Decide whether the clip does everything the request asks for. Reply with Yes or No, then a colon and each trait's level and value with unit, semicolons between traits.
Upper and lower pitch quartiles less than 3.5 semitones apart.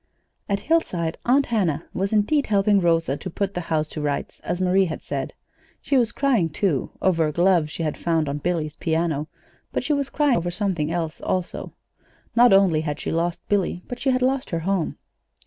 No: average, 4.6 semitones